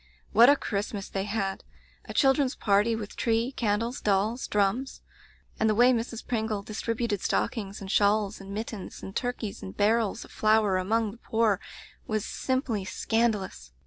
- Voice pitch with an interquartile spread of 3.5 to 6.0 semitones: No, narrow, 2.5 semitones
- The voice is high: Yes, high, 215 Hz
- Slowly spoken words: No, average, 160 wpm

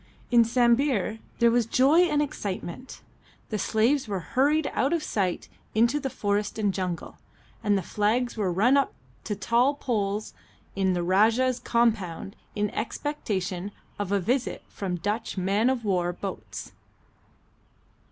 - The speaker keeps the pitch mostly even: No, average, 4.3 semitones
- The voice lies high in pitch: Yes, high, 220 Hz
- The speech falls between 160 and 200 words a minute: No, average, 140 wpm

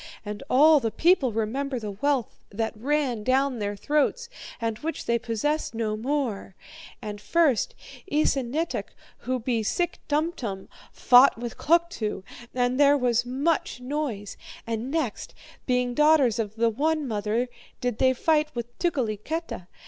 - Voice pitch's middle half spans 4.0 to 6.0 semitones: Yes, average, 4.9 semitones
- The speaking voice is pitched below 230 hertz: No, very high, 250 Hz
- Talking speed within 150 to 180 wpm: No, average, 140 wpm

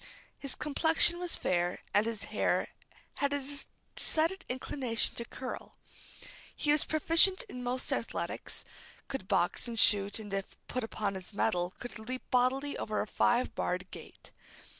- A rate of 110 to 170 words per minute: Yes, average, 150 wpm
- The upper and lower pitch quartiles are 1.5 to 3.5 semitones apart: No, wide, 5.6 semitones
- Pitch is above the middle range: Yes, high, 245 Hz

